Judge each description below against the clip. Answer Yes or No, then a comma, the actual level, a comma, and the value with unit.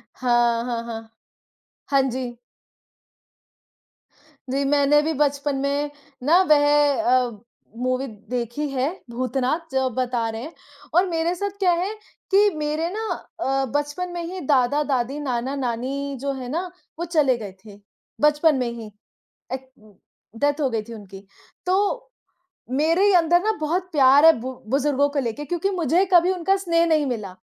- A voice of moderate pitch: No, very high, 285 Hz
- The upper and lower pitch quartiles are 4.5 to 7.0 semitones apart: Yes, average, 4.8 semitones